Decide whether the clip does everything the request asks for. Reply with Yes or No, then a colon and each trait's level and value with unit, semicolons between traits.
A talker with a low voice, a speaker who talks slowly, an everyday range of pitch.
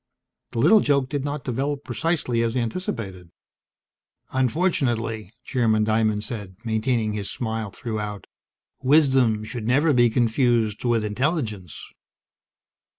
Yes: low, 115 Hz; slow, 110 wpm; average, 3.7 semitones